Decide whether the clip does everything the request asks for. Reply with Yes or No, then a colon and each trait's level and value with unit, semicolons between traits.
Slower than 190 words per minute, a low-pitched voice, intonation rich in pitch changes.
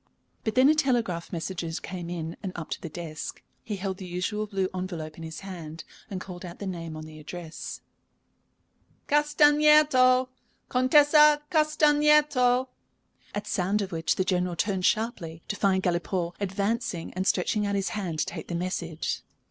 No: average, 165 wpm; high, 190 Hz; wide, 6.5 semitones